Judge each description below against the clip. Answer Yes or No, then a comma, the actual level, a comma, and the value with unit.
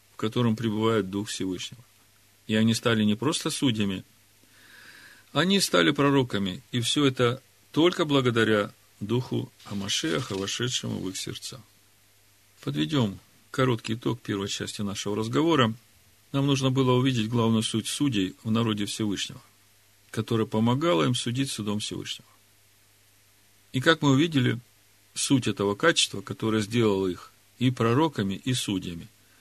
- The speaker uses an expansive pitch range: No, average, 4.1 semitones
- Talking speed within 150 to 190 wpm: No, average, 125 wpm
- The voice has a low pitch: Yes, low, 110 Hz